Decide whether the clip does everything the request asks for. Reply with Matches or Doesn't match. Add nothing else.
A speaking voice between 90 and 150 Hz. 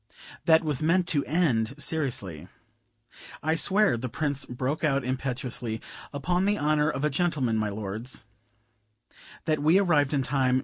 Matches